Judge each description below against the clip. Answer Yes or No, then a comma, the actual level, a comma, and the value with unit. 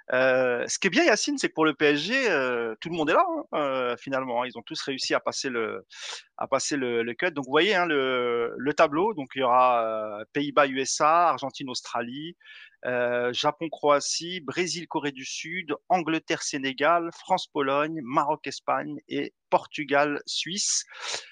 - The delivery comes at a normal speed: Yes, average, 180 wpm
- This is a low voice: No, medium, 145 Hz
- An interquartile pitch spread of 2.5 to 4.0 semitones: No, average, 4.5 semitones